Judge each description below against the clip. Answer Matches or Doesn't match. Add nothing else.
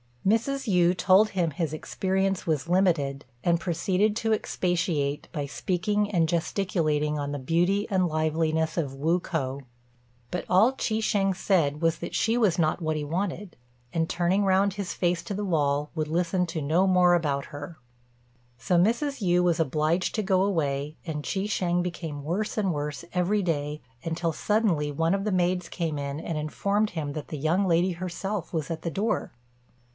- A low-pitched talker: Doesn't match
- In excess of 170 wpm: Matches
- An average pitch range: Matches